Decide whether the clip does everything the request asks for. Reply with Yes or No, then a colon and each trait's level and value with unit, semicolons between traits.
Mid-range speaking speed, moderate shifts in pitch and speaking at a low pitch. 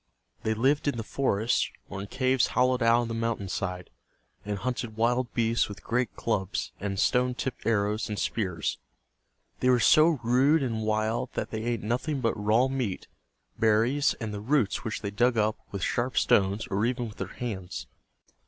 Yes: average, 180 wpm; average, 3.2 semitones; low, 115 Hz